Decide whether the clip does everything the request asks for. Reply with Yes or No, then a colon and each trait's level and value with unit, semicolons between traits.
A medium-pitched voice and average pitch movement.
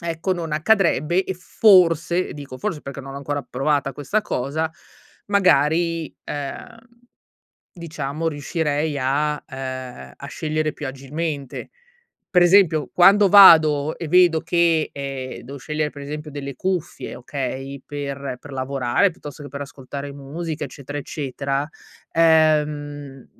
Yes: medium, 150 Hz; average, 3.1 semitones